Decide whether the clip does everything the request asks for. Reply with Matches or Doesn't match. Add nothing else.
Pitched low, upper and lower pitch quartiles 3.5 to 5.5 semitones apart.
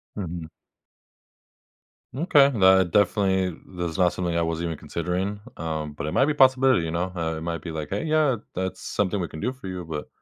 Matches